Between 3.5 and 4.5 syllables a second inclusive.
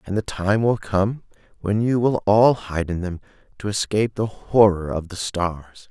Yes: 4.4 syllables/s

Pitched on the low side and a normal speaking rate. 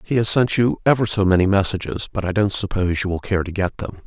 No: low, 100 Hz; fast, 265 wpm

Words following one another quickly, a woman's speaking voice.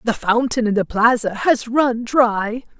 No: average, 170 wpm; female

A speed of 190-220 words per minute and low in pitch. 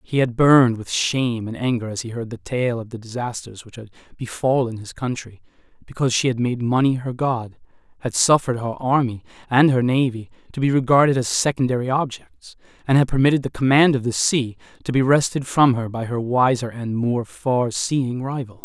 Yes: average, 195 wpm; low, 125 Hz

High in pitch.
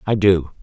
No: very low, 95 Hz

